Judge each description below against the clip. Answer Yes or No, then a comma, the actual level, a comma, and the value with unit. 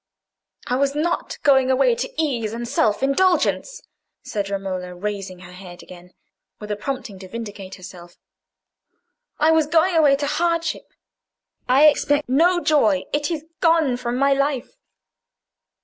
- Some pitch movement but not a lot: No, wide, 7.3 semitones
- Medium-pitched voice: No, very high, 265 Hz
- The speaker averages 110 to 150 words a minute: Yes, average, 145 wpm